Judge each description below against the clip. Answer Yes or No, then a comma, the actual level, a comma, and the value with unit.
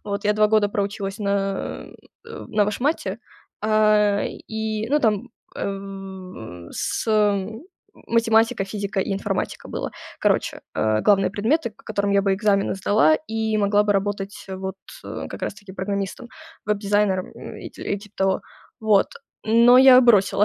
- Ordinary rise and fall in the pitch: No, narrow, 1.7 semitones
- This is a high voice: Yes, high, 205 Hz